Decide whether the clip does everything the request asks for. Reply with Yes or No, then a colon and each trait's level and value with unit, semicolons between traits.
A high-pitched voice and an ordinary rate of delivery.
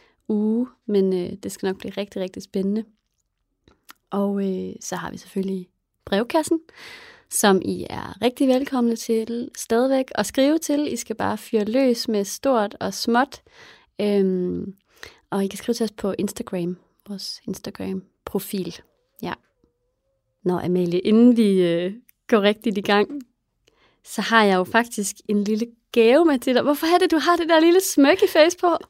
Yes: high, 220 Hz; average, 160 wpm